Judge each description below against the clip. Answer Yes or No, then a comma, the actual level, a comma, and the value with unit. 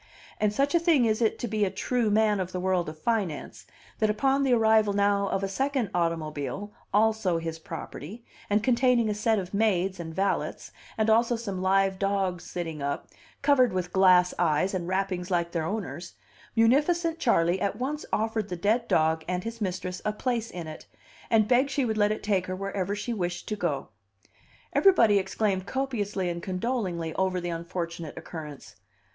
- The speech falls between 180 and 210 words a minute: Yes, average, 185 wpm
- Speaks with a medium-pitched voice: No, high, 200 Hz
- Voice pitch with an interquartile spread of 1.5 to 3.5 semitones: No, average, 4.0 semitones